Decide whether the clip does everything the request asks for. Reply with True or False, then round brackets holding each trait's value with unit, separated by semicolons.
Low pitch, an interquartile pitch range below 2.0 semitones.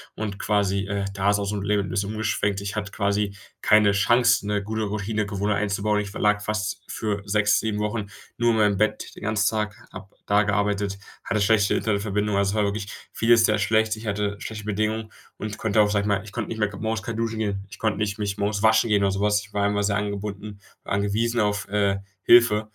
True (105 Hz; 1.2 semitones)